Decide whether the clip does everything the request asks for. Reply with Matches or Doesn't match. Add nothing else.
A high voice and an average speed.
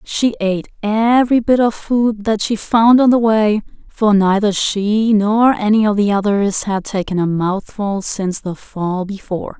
Matches